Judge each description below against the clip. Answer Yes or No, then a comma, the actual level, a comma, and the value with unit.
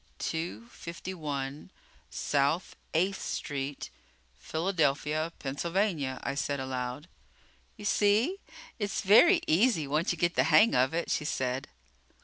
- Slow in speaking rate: Yes, slow, 125 wpm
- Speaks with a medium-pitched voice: Yes, medium, 160 Hz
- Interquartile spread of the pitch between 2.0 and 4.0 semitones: No, wide, 5.4 semitones